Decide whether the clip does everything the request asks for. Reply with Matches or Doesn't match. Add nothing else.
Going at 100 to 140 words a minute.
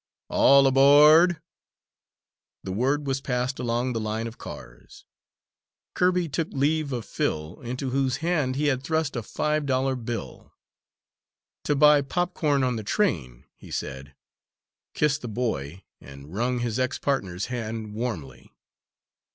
Matches